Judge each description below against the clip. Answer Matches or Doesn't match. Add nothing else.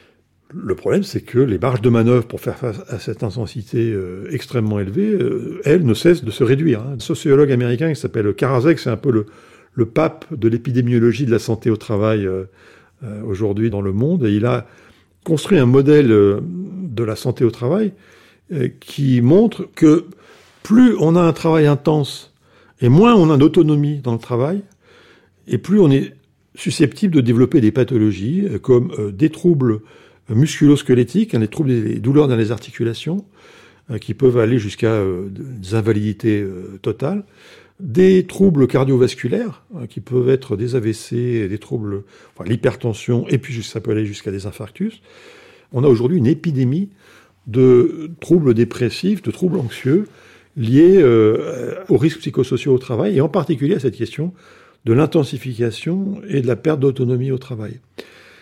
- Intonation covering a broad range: Matches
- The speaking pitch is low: Matches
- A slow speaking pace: Doesn't match